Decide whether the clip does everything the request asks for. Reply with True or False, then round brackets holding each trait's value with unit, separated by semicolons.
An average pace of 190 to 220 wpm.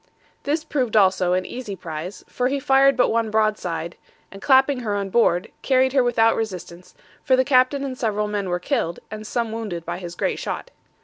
True (195 wpm)